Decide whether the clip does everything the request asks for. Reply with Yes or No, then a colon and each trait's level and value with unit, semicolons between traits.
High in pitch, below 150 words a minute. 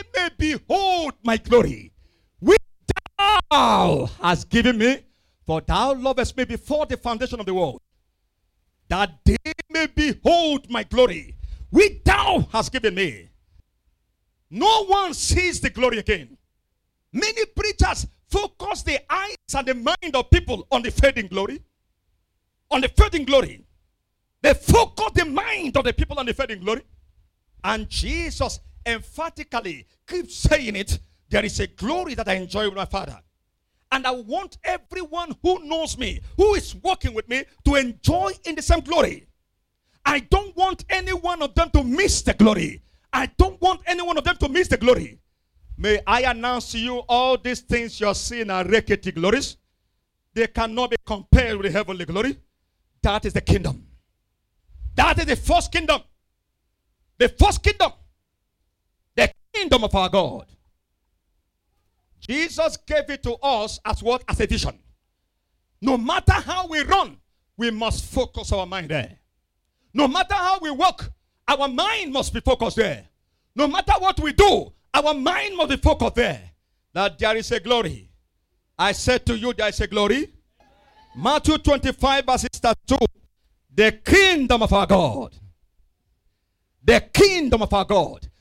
No: high, 245 Hz; average, 155 wpm